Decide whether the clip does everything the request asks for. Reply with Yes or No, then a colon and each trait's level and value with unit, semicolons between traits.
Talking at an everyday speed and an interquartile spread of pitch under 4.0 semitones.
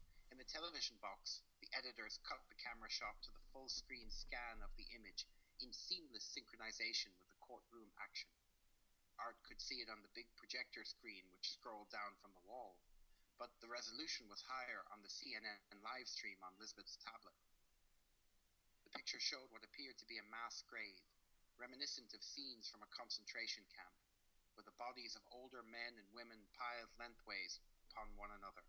Yes: average, 170 wpm; average, 3.3 semitones